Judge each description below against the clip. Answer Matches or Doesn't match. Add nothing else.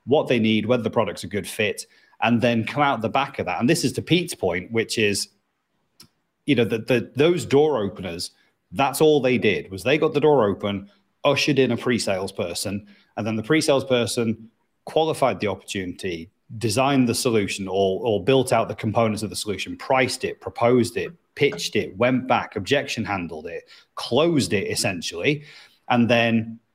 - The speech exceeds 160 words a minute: Matches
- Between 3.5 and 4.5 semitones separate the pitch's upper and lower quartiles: Matches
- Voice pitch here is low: Matches